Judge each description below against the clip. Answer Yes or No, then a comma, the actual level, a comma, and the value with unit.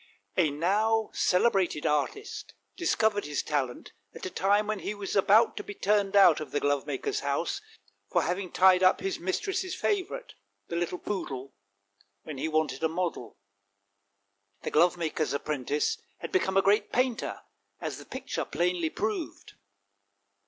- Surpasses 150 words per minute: No, average, 145 wpm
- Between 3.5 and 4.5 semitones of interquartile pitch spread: No, wide, 5.4 semitones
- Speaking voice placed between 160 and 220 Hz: Yes, medium, 185 Hz